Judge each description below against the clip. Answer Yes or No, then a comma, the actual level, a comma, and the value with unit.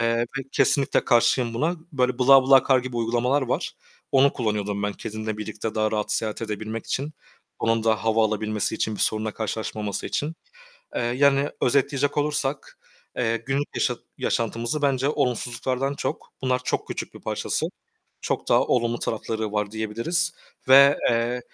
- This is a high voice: No, low, 120 Hz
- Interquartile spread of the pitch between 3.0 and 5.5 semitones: Yes, average, 3.7 semitones